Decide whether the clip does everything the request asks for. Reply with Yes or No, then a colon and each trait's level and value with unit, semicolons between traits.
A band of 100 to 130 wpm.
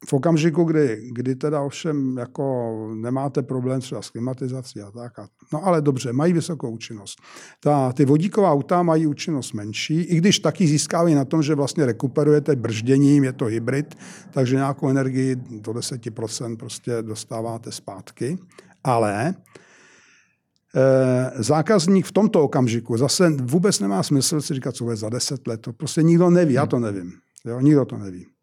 No: average, 165 wpm